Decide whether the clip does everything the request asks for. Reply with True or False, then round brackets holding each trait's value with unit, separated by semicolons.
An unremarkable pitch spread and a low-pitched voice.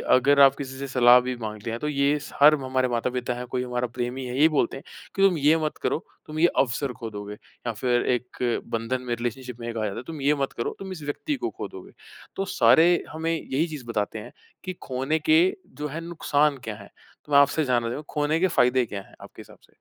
True (3.7 semitones; 130 Hz)